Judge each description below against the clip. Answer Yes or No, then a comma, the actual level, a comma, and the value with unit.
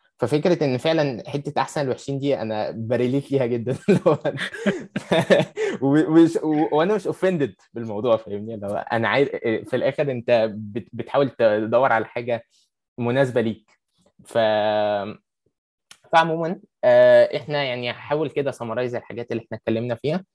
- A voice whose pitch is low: Yes, low, 130 Hz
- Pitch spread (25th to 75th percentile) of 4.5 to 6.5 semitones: Yes, average, 4.8 semitones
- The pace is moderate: Yes, average, 110 wpm